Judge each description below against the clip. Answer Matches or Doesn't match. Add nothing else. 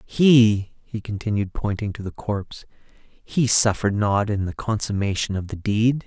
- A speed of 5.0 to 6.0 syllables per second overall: Doesn't match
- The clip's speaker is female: Doesn't match